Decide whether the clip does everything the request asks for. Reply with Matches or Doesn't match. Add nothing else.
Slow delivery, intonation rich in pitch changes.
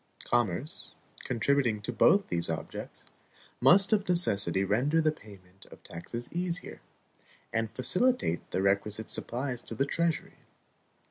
Matches